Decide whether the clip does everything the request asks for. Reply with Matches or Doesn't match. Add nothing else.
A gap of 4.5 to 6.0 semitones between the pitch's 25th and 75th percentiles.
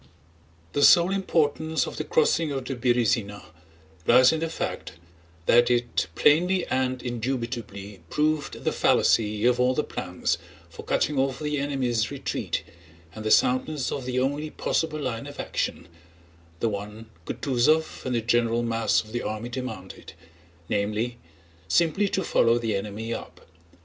Matches